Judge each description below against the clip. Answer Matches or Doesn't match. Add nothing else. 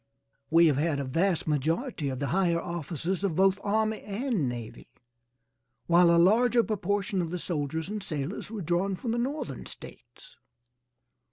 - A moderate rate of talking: Matches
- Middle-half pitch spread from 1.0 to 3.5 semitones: Doesn't match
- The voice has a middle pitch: Matches